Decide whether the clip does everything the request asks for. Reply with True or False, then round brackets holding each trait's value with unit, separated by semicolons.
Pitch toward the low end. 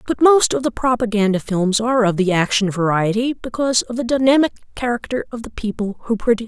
False (230 Hz)